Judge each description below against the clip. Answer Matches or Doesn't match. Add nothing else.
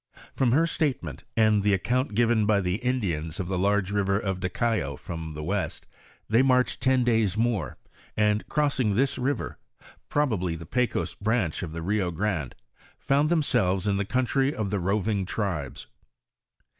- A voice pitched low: Matches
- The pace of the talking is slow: Doesn't match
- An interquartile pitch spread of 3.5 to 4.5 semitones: Doesn't match